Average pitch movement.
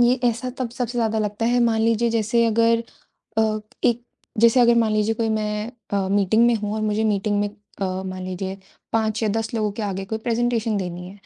No: narrow, 2.1 semitones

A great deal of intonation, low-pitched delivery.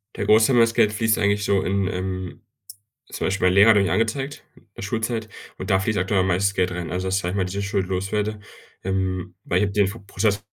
No: narrow, 2.5 semitones; low, 100 Hz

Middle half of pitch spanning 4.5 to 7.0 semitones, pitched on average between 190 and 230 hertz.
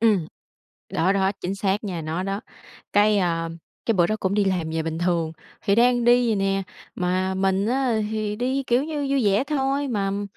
No: average, 4.1 semitones; high, 200 Hz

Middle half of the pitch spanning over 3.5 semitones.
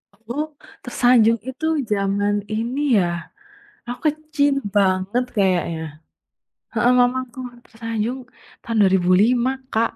Yes: average, 4.1 semitones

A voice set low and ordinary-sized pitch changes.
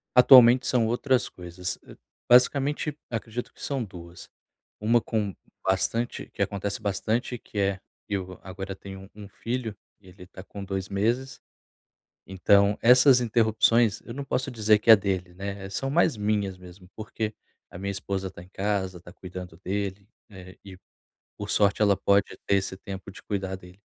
Yes: low, 100 Hz; average, 3.3 semitones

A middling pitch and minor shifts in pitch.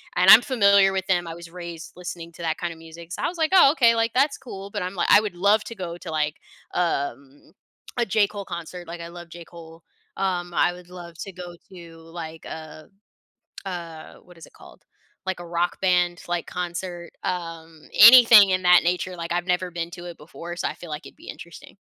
Yes: medium, 175 Hz; narrow, 2.3 semitones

